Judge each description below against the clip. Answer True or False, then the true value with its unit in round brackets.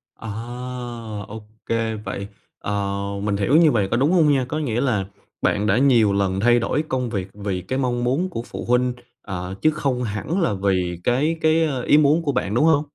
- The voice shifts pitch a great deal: True (6.0 semitones)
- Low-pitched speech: True (120 Hz)